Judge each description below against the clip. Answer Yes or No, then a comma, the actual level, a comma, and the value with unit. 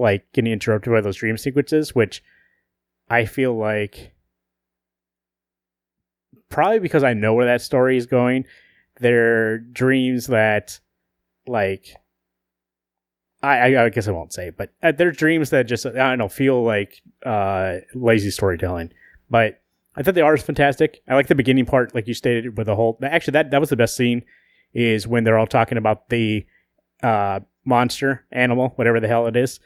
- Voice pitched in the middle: No, low, 115 Hz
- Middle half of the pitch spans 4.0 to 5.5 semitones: Yes, average, 4.9 semitones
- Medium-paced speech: Yes, average, 170 wpm